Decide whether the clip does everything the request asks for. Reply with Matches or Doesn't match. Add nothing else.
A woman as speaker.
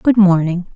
Matches